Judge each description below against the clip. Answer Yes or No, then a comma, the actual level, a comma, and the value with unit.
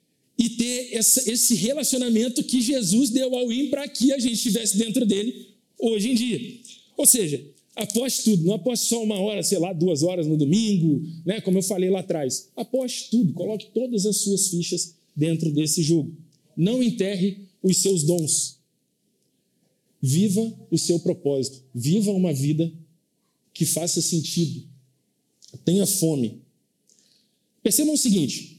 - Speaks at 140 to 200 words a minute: Yes, average, 150 wpm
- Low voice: No, high, 200 Hz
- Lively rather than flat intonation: Yes, wide, 5.8 semitones